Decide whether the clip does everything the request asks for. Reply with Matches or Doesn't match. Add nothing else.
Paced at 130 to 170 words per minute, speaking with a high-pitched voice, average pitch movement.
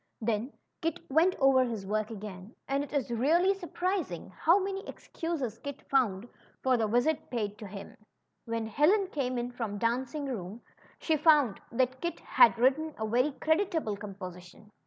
Doesn't match